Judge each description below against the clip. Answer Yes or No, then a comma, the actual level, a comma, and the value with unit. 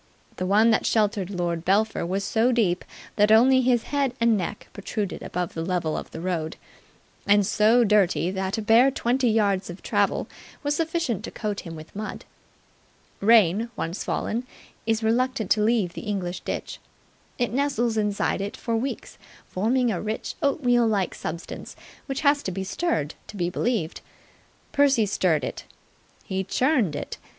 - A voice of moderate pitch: No, high, 215 Hz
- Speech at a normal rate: Yes, average, 165 wpm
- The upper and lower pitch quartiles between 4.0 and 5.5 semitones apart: Yes, average, 4.4 semitones